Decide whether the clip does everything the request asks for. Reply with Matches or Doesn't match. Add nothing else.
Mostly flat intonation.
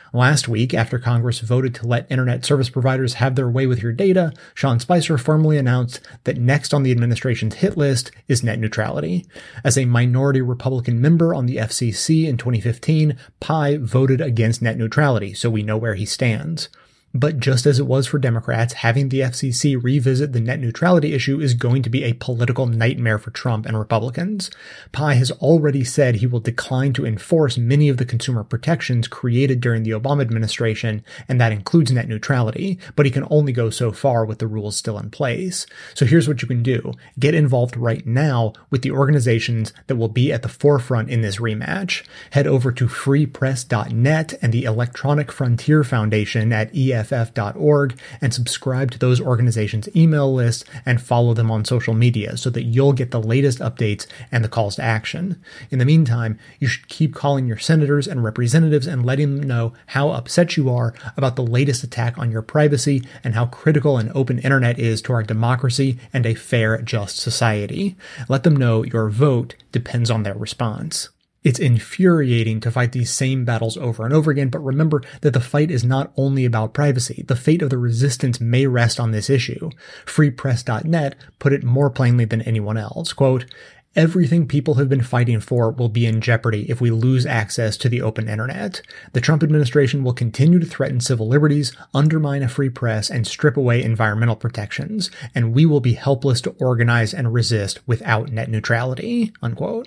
Doesn't match